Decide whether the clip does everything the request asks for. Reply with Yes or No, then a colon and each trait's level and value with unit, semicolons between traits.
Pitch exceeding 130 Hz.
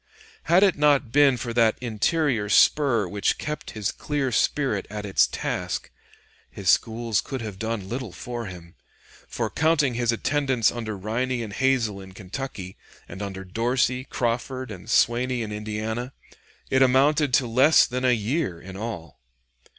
No: low, 120 Hz